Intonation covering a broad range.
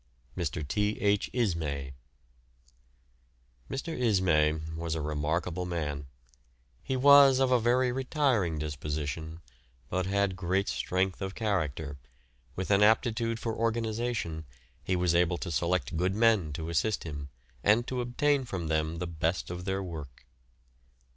Yes: wide, 6.1 semitones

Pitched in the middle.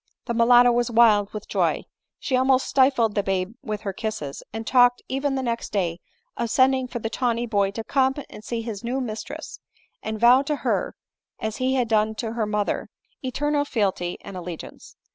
No: high, 230 Hz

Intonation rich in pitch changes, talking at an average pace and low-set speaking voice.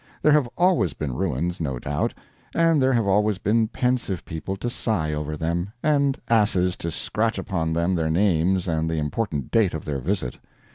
Yes: wide, 6.0 semitones; average, 185 wpm; very low, 95 Hz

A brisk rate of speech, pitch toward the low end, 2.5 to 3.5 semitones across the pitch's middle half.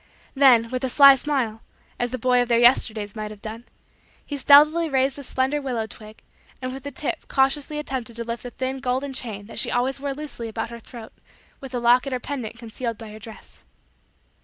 No: fast, 210 wpm; very high, 250 Hz; average, 2.9 semitones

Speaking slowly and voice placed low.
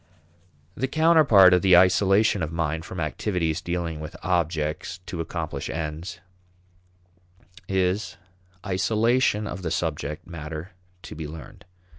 Yes: slow, 120 wpm; very low, 90 Hz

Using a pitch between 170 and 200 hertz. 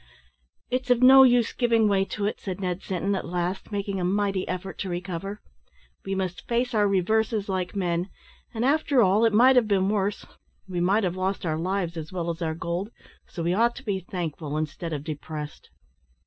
Yes: high, 190 Hz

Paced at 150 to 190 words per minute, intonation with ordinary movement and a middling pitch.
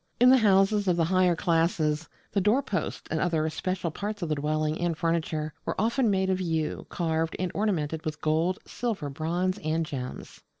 Yes: average, 180 wpm; average, 3.5 semitones; medium, 170 Hz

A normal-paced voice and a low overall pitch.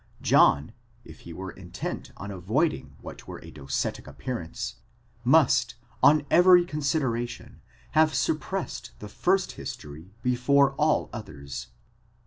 No: slow, 115 wpm; low, 125 Hz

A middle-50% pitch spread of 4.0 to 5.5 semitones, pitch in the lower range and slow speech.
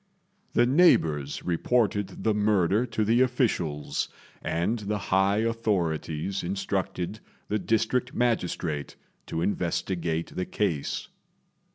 Yes: average, 4.8 semitones; low, 100 Hz; slow, 100 wpm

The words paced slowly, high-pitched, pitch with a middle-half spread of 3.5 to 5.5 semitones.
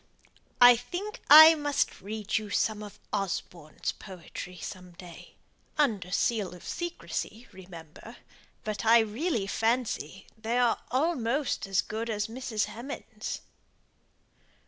Yes: slow, 120 wpm; high, 220 Hz; average, 4.3 semitones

